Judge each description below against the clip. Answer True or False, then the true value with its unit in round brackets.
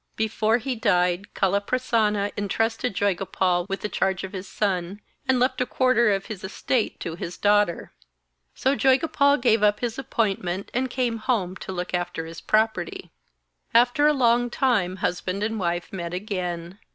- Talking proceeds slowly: False (160 wpm)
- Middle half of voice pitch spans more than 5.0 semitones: False (4.6 semitones)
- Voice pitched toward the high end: True (205 Hz)